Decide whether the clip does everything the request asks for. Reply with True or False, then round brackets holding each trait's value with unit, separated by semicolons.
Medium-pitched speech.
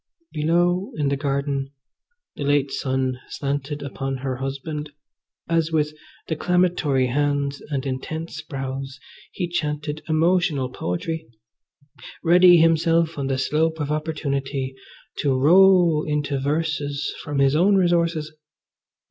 True (150 Hz)